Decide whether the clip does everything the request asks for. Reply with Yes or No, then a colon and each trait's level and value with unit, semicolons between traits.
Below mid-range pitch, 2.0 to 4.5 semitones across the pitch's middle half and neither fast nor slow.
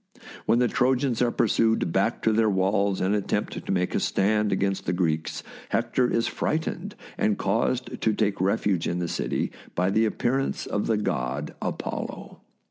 Yes: low, 105 Hz; average, 3.5 semitones; average, 170 wpm